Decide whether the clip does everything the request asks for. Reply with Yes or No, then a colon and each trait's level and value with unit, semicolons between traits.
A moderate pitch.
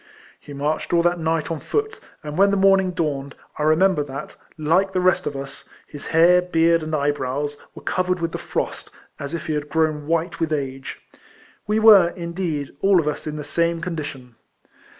Yes: medium, 165 Hz